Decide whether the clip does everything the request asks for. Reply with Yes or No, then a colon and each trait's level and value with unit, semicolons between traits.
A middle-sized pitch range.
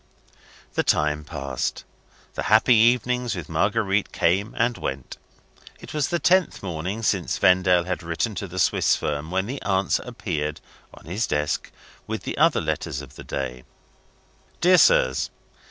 No: wide, 7.0 semitones